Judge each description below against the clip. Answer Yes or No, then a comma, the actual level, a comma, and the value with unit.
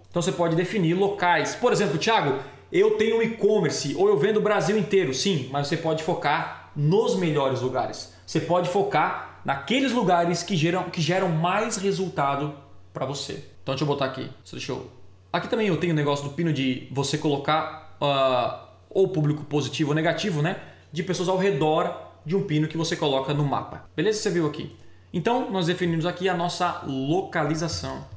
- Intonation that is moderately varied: Yes, average, 4.6 semitones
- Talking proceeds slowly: No, fast, 185 wpm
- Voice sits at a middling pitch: Yes, medium, 165 Hz